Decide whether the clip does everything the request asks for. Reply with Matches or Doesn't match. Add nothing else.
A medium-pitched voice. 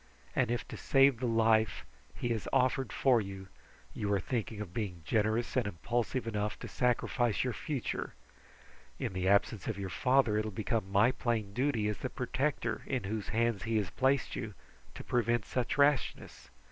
Doesn't match